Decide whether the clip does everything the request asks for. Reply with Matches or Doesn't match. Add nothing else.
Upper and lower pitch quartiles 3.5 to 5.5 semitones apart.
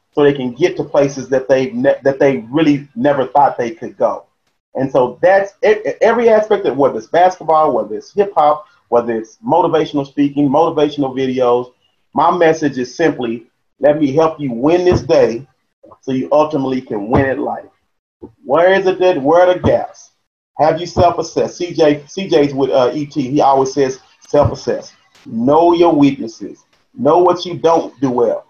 Matches